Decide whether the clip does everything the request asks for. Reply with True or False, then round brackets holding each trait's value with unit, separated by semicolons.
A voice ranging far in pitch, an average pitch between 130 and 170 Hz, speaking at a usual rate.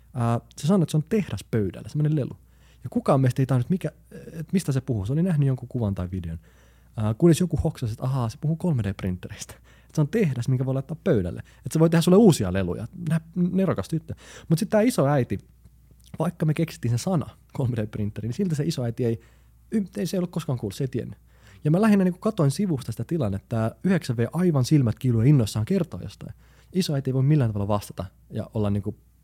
False (6.9 semitones; 135 Hz; 215 wpm)